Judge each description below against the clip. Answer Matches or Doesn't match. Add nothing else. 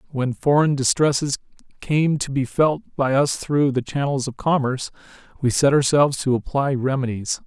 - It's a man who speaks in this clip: Matches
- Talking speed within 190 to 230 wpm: Doesn't match